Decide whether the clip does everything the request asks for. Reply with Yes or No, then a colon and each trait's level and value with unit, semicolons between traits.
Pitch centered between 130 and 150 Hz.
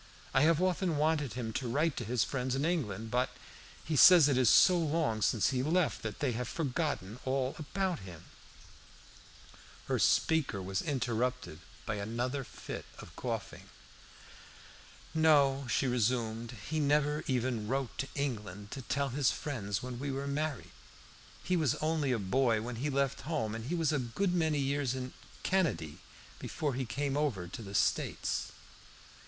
Yes: low, 135 Hz